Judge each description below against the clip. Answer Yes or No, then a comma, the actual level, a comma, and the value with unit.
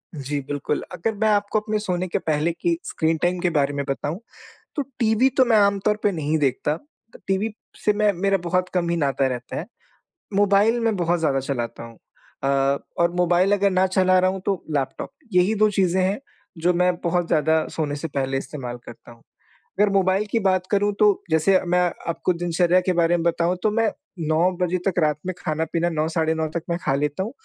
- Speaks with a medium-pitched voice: Yes, medium, 175 Hz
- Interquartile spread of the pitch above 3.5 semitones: Yes, average, 4.1 semitones